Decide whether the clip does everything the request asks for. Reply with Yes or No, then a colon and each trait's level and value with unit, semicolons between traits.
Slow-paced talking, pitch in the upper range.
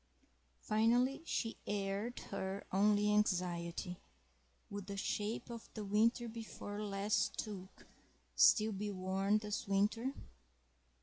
Yes: slow, 105 wpm; high, 210 Hz